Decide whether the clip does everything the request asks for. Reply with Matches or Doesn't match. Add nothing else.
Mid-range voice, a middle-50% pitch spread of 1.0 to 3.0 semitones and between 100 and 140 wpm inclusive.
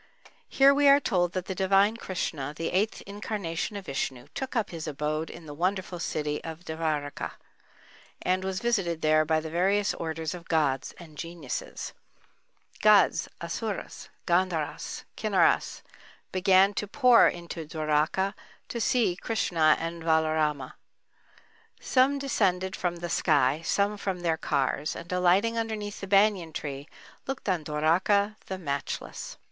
Doesn't match